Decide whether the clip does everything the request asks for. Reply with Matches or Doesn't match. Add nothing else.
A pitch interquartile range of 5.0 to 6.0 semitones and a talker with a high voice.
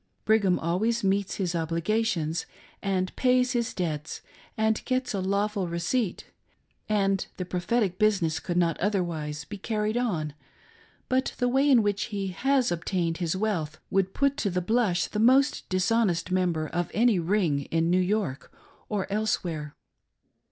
Doesn't match